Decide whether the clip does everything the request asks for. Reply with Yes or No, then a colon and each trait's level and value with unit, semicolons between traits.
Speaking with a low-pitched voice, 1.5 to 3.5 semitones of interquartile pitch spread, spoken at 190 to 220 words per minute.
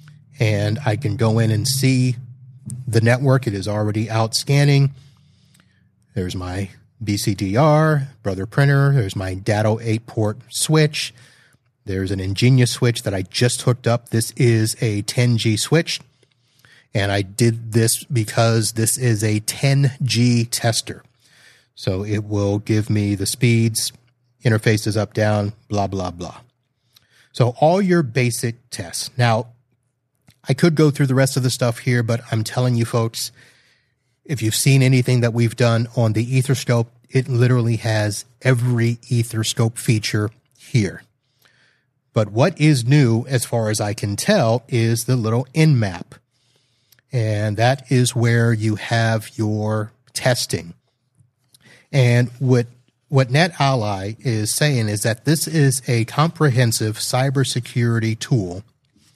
No: low, 120 Hz; average, 2.8 semitones; average, 140 wpm